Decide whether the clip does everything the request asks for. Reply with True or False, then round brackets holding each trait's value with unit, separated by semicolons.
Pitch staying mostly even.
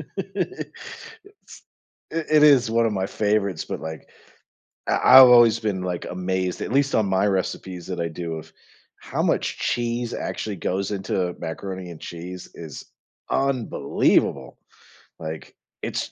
False (5.0 semitones)